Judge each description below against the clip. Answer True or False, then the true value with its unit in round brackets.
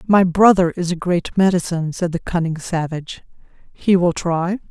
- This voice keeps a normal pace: True (165 wpm)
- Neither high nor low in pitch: True (175 Hz)